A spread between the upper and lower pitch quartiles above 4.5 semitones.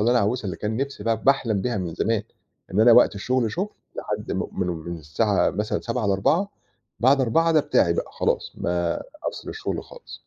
Yes: average, 4.9 semitones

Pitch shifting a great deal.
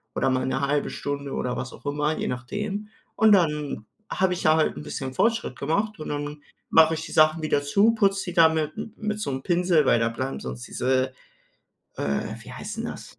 Yes: wide, 6.0 semitones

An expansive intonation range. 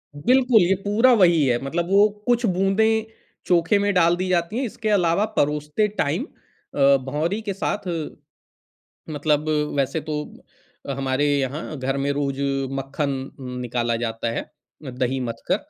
Yes: wide, 6.6 semitones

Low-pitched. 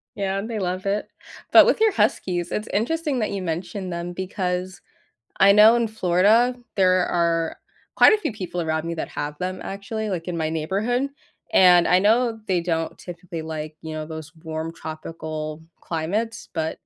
No: medium, 180 Hz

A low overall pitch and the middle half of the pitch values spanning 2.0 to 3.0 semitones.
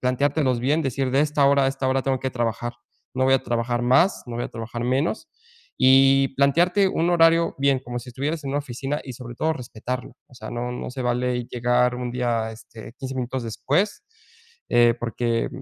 Yes: low, 130 Hz; narrow, 2.5 semitones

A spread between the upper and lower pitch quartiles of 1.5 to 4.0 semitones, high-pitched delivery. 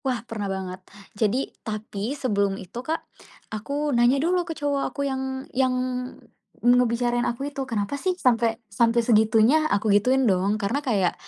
No: average, 4.4 semitones; high, 240 Hz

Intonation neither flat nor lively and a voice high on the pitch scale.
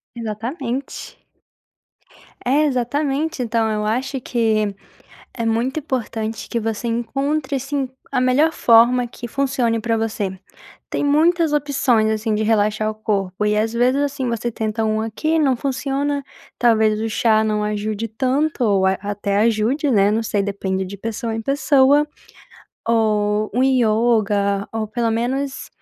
Yes: average, 3.7 semitones; high, 230 Hz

